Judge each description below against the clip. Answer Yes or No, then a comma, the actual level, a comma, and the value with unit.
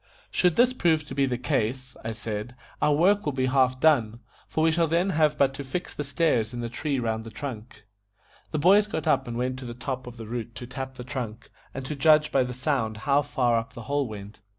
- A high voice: No, low, 130 Hz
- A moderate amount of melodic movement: Yes, average, 4.2 semitones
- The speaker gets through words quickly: Yes, fast, 245 wpm